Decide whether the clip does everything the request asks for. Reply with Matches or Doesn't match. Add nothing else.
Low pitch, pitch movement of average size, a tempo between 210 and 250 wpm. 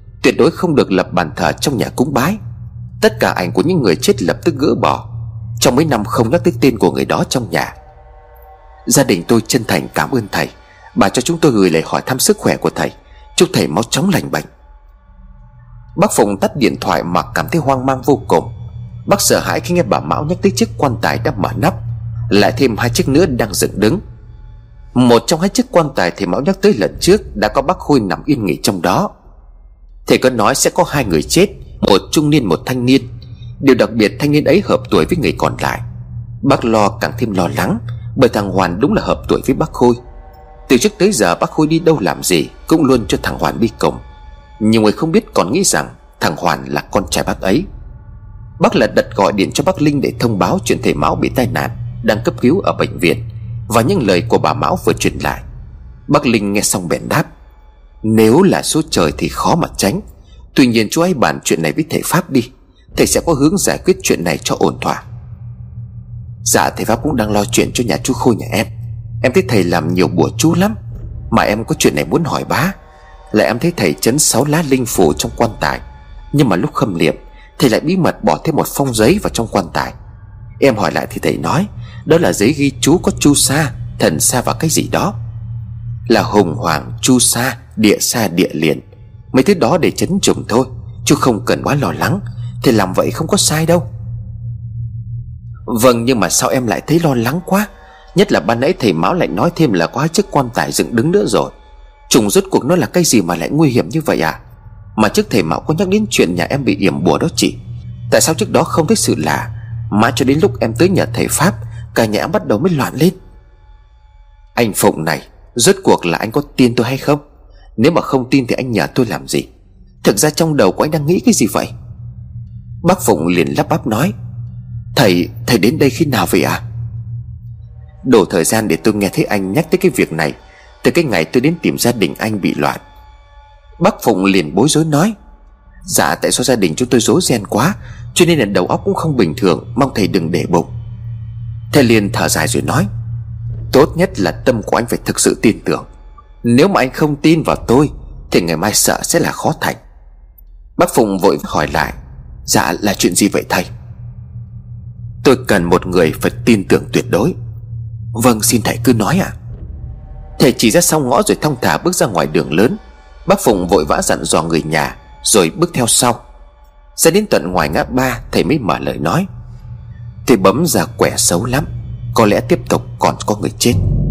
Matches